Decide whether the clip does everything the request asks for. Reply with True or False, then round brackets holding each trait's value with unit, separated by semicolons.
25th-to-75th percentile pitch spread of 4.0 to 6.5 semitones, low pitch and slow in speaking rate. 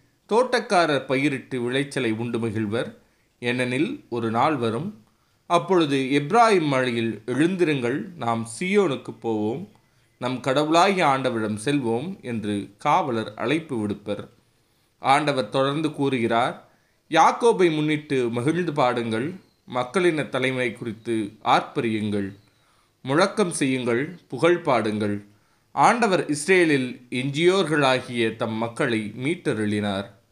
False (4.8 semitones; 125 Hz; 90 wpm)